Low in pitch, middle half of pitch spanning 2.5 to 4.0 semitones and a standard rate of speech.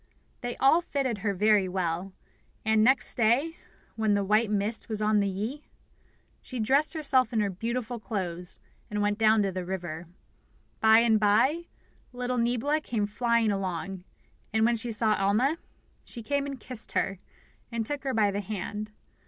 No: high, 220 Hz; average, 3.5 semitones; average, 170 wpm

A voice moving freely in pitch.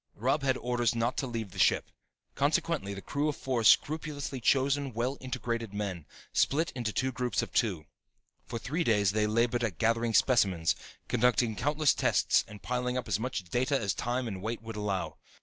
No: average, 3.6 semitones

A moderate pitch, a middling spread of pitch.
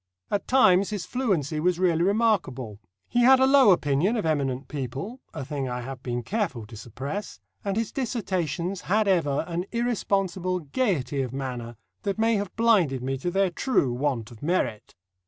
No: medium, 175 Hz; wide, 7.6 semitones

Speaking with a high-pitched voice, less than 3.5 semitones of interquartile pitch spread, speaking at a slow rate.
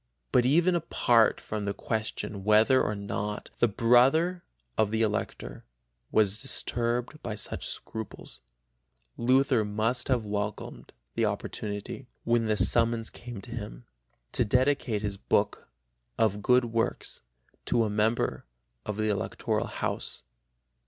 No: low, 115 Hz; average, 2.7 semitones; slow, 130 wpm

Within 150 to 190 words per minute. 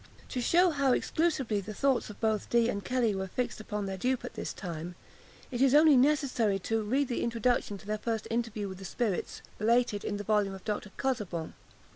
No: fast, 205 wpm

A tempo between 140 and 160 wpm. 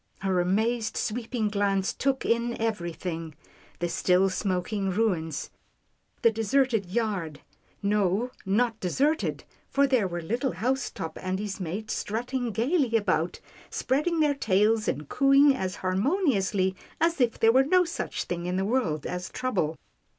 Yes: average, 150 wpm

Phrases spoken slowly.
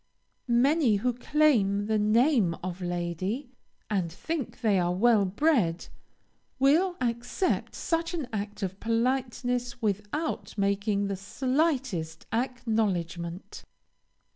Yes: slow, 105 wpm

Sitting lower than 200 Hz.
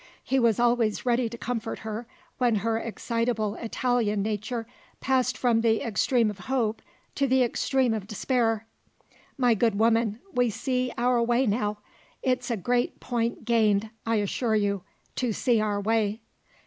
No: high, 230 Hz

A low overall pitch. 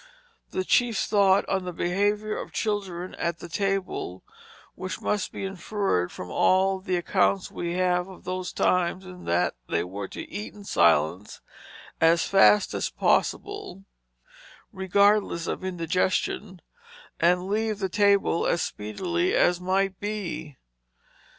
No: medium, 185 Hz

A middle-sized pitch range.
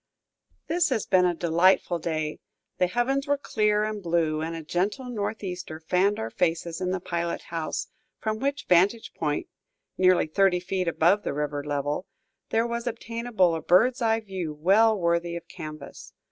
Yes: average, 4.7 semitones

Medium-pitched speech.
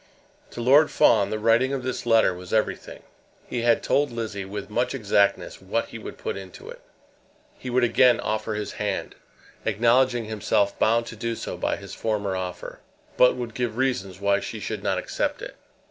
No: low, 110 Hz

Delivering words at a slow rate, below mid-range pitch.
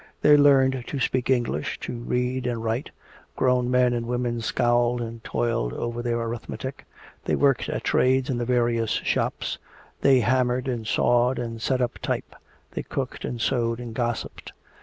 No: average, 165 wpm; low, 120 Hz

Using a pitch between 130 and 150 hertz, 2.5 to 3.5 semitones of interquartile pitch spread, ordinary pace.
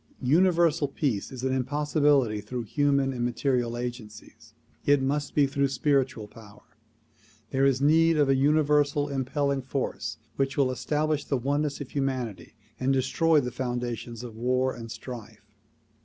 Yes: low, 135 Hz; average, 2.9 semitones; average, 145 wpm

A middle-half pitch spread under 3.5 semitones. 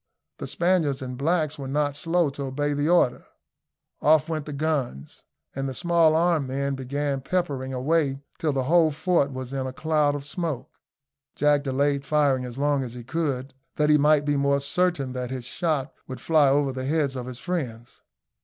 Yes: average, 2.8 semitones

